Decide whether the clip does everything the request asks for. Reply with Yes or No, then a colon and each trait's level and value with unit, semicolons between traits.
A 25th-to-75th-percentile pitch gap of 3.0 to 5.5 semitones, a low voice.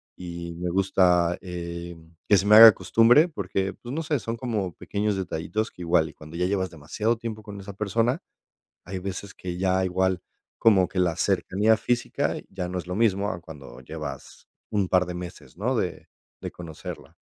Yes: average, 3.3 semitones; very low, 95 Hz